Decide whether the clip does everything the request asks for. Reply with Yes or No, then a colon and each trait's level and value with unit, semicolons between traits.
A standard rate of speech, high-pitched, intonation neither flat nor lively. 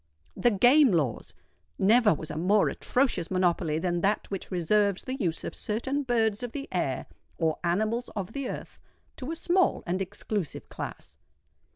No: average, 165 wpm; high, 205 Hz; wide, 5.7 semitones